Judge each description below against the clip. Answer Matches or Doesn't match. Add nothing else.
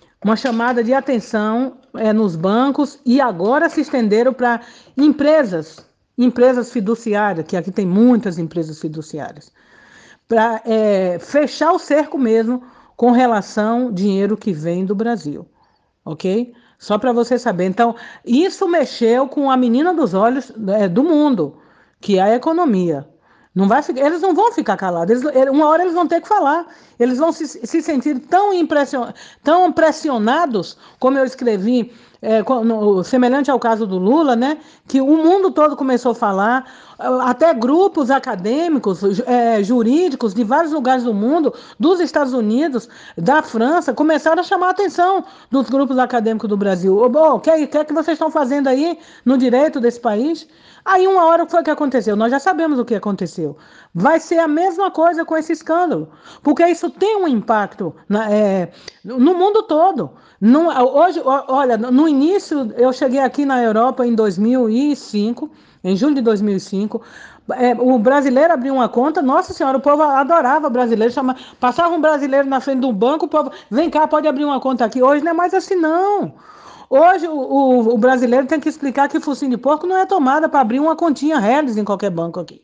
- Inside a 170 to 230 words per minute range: Matches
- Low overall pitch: Doesn't match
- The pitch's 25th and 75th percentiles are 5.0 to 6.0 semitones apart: Matches